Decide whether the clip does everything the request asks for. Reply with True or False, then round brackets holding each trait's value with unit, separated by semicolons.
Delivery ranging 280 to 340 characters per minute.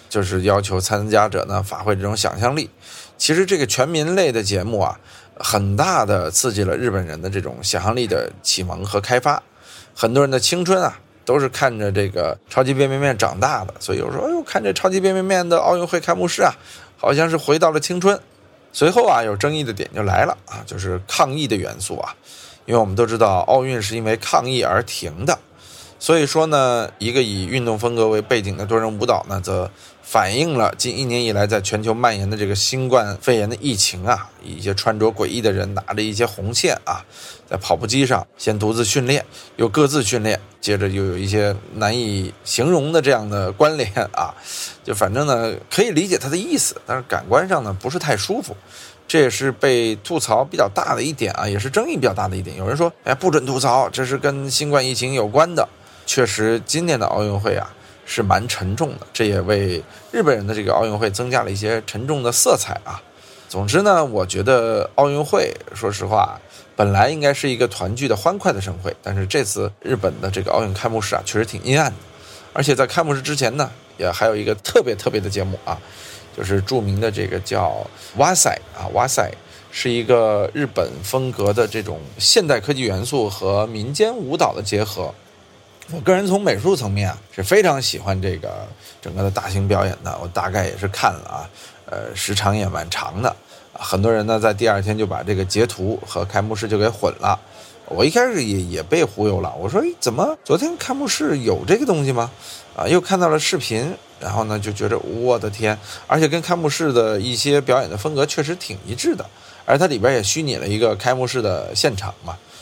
True (310 characters per minute)